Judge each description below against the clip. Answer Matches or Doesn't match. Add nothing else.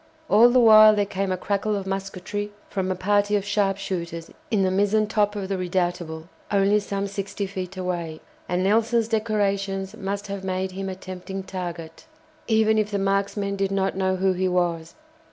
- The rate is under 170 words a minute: Doesn't match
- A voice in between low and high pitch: Doesn't match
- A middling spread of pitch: Doesn't match